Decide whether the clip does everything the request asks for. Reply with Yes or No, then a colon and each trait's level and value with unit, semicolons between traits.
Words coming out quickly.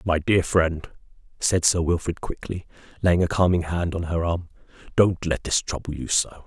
No: average, 185 wpm